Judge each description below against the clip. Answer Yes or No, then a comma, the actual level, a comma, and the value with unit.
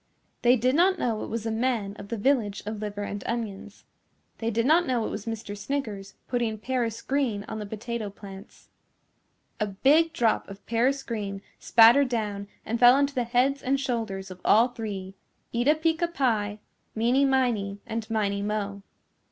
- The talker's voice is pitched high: Yes, high, 225 Hz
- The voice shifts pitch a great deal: No, average, 3.8 semitones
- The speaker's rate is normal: Yes, average, 175 wpm